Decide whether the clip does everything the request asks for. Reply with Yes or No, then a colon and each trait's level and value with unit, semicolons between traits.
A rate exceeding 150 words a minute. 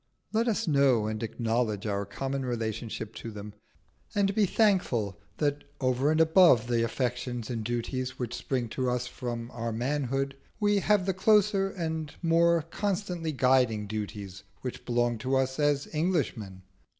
No: average, 145 wpm